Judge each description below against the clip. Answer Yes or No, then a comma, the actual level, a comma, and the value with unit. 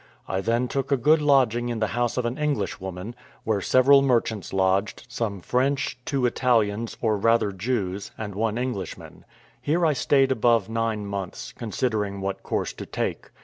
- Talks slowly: No, average, 165 wpm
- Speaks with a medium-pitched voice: No, low, 115 Hz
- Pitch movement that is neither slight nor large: Yes, average, 4.1 semitones